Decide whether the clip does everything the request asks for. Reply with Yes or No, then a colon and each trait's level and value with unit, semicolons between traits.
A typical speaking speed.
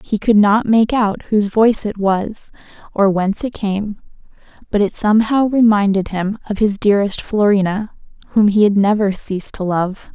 Yes: average, 170 wpm